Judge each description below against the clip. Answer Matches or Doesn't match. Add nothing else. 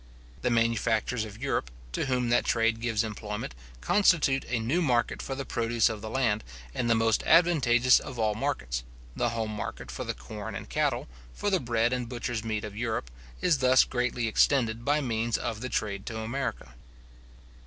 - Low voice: Matches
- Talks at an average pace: Matches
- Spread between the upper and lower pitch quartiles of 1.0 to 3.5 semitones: Matches